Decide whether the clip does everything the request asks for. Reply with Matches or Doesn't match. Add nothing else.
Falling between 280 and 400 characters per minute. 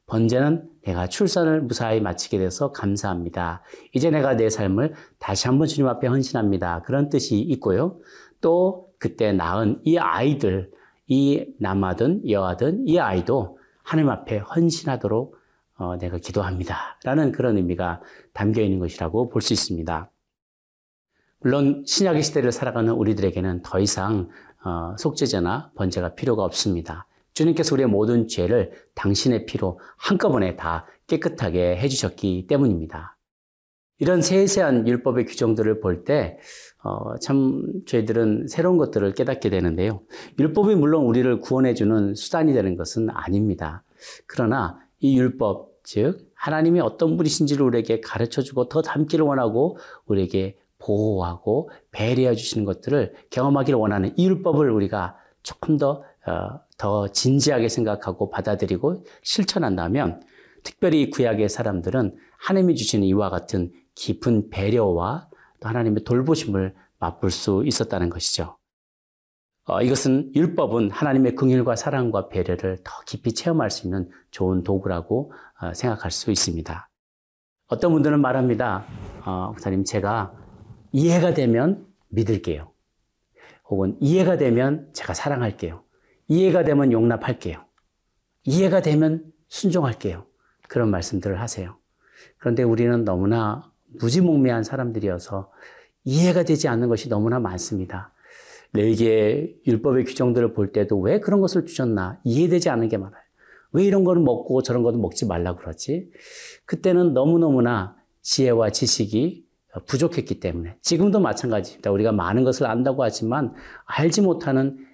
Matches